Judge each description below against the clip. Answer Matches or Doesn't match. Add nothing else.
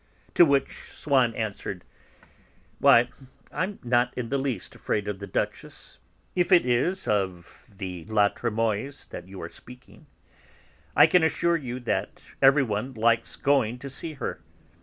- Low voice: Matches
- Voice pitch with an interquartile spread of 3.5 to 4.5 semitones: Doesn't match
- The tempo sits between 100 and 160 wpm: Matches